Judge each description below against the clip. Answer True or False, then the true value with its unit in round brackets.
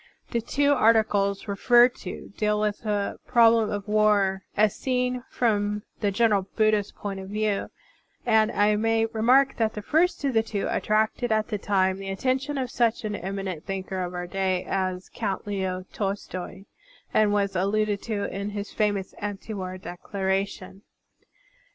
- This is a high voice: True (210 Hz)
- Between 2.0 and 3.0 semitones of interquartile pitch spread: True (2.4 semitones)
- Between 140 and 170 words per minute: True (160 wpm)